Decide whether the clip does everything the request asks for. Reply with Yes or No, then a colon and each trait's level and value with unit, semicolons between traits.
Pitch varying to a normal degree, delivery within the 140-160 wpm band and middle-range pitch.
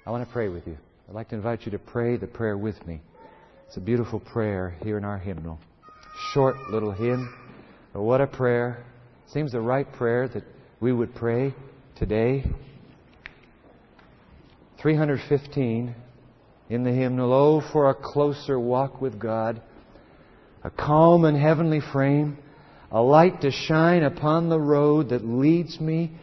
No: average, 4.4 semitones; average, 155 wpm; low, 125 Hz